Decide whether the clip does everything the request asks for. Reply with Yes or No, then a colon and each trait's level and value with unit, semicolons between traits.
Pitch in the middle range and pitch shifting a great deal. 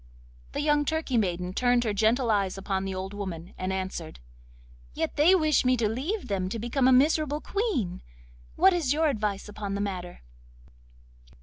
No: high, 220 Hz; wide, 7.3 semitones